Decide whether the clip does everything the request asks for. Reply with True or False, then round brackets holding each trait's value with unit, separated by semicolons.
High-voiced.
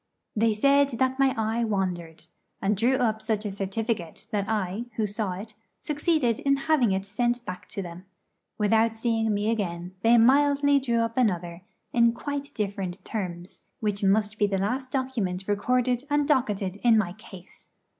True (220 Hz)